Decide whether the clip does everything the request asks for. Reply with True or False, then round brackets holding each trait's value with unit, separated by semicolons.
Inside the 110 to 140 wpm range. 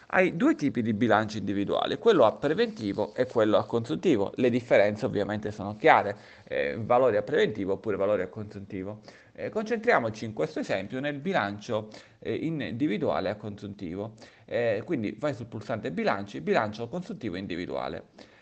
False (155 wpm)